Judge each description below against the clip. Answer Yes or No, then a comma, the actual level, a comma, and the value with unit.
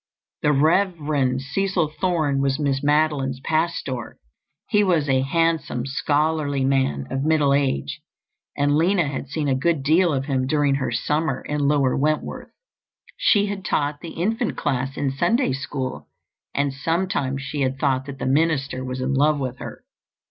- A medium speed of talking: Yes, average, 160 wpm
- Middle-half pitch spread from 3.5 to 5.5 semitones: No, average, 2.9 semitones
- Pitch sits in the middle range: Yes, medium, 145 Hz